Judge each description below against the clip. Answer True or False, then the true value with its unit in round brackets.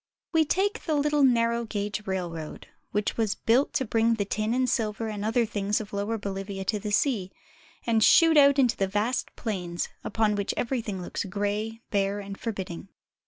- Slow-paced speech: False (175 wpm)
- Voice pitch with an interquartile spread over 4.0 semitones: False (2.8 semitones)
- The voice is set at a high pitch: True (215 Hz)